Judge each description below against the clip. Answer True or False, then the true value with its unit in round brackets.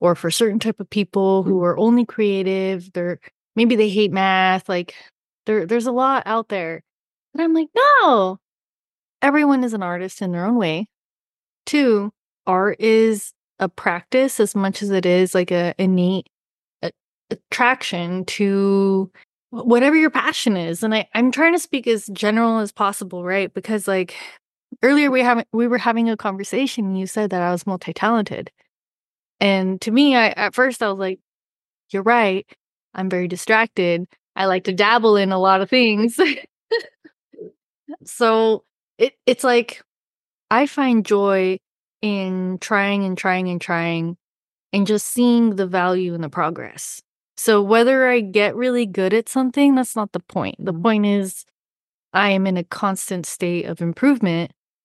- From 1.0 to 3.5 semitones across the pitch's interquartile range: False (4.1 semitones)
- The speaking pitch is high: True (205 Hz)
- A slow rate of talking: False (160 wpm)